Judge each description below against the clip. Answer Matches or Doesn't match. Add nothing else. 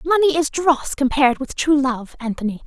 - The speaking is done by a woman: Matches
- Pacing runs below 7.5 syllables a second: Matches